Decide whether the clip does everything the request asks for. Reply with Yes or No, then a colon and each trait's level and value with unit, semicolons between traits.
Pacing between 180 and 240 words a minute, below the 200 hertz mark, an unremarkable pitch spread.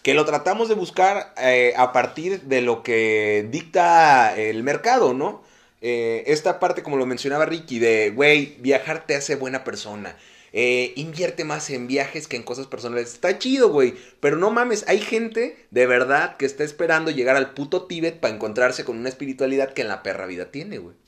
No: fast, 190 wpm; medium, 140 Hz; wide, 5.9 semitones